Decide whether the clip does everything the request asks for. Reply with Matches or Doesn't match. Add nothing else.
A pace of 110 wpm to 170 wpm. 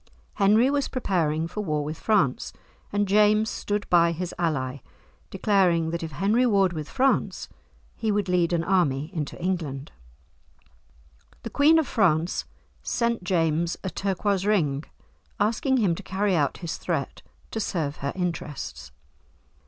Matches